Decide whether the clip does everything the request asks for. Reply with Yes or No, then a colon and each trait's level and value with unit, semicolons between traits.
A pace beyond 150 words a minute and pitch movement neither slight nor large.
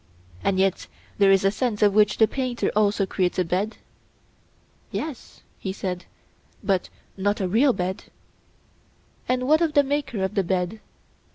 Yes: average, 160 wpm; average, 4.6 semitones